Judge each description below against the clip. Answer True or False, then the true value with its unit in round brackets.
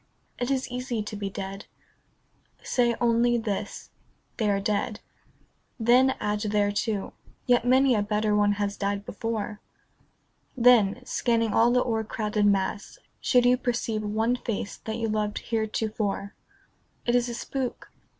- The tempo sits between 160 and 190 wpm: False (145 wpm)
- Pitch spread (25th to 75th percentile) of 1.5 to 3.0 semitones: True (2.7 semitones)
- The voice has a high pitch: True (220 Hz)